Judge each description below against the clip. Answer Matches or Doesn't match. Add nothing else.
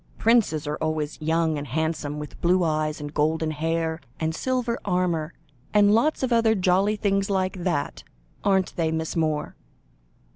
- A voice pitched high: Doesn't match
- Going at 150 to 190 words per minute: Matches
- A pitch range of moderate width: Matches